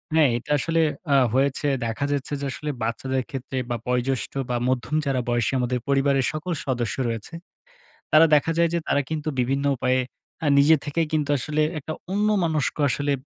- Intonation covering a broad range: No, average, 3.3 semitones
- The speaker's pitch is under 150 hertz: Yes, medium, 140 Hz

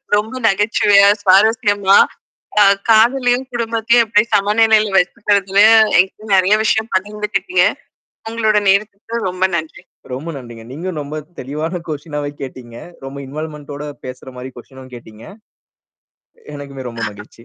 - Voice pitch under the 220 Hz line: Yes, high, 190 Hz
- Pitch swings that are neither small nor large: No, wide, 7.1 semitones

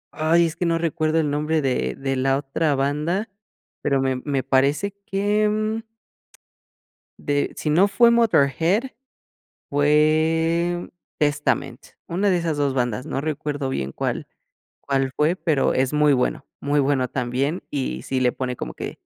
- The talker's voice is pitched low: No, medium, 150 Hz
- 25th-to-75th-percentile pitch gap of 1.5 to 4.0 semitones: Yes, average, 3.7 semitones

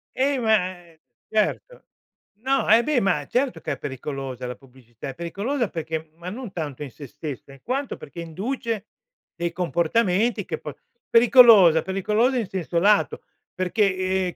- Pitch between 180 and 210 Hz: Yes, medium, 185 Hz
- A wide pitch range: Yes, wide, 6.7 semitones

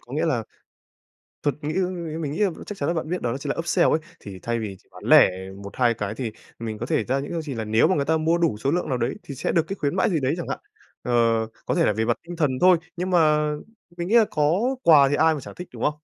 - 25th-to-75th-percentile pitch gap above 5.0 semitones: Yes, wide, 5.6 semitones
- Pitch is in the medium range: Yes, medium, 150 Hz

